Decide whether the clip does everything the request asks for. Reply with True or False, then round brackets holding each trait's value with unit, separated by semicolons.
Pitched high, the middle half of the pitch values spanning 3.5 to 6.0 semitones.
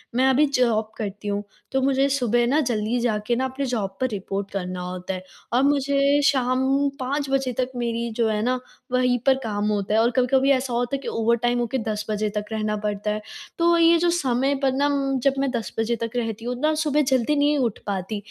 True (245 Hz; 4.1 semitones)